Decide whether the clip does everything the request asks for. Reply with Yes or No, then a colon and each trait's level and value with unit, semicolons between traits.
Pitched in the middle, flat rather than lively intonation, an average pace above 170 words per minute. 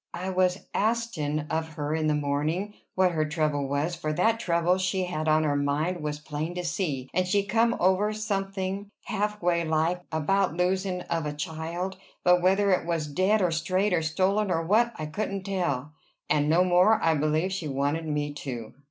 No: medium, 175 Hz; average, 3.7 semitones; average, 190 wpm